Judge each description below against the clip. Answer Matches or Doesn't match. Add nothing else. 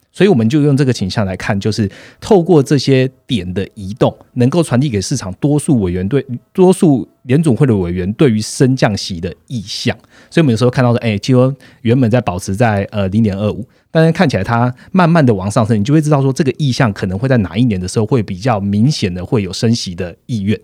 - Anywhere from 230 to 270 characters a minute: Doesn't match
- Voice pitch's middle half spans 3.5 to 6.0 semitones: Matches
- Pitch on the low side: Matches